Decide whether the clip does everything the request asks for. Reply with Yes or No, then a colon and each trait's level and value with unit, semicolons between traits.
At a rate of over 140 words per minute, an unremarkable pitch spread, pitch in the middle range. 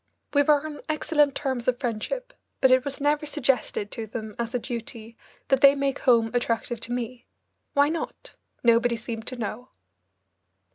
No: average, 170 wpm; average, 3.5 semitones; very high, 250 Hz